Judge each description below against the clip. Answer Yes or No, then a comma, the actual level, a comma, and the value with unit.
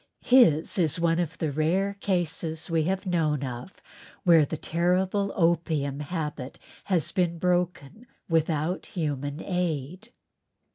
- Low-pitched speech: No, medium, 165 Hz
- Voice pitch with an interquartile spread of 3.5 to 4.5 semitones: No, average, 3.0 semitones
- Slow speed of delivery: Yes, slow, 125 wpm